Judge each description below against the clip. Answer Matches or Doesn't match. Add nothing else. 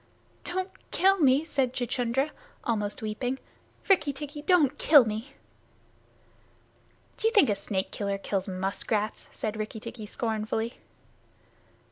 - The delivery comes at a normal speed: Doesn't match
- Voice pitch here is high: Matches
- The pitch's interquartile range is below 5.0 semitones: Doesn't match